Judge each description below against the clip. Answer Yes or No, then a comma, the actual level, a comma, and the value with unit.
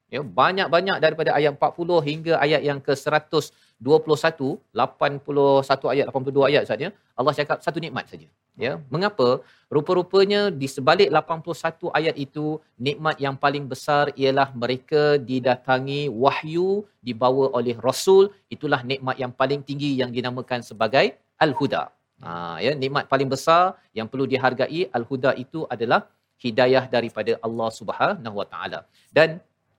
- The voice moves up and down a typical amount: Yes, average, 3.4 semitones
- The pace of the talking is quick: Yes, fast, 130 wpm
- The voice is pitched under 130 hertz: No, medium, 140 Hz